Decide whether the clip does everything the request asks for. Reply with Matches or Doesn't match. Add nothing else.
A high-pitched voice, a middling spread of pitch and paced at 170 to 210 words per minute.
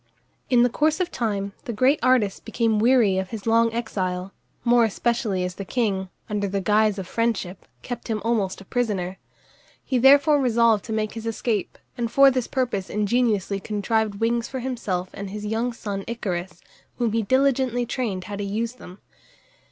Matches